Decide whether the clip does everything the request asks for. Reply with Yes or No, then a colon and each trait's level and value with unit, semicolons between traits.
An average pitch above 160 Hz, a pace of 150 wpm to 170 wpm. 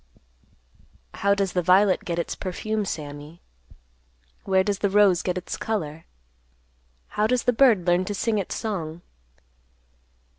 No: high, 190 Hz; average, 140 wpm